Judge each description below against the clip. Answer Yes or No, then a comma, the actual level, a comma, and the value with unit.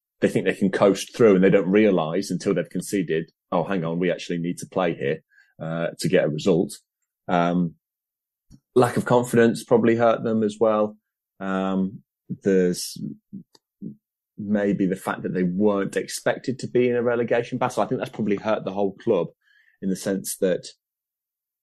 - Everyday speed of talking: Yes, average, 175 wpm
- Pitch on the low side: Yes, low, 100 Hz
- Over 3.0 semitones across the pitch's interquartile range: Yes, average, 4.0 semitones